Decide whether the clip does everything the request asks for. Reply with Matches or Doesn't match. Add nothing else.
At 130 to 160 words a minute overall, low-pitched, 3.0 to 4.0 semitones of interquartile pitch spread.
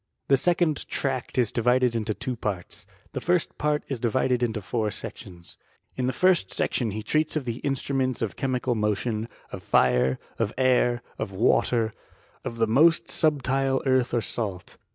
Doesn't match